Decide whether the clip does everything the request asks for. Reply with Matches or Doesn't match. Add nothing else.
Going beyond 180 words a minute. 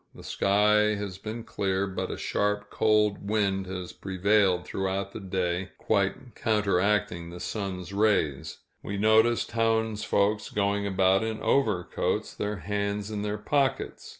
Doesn't match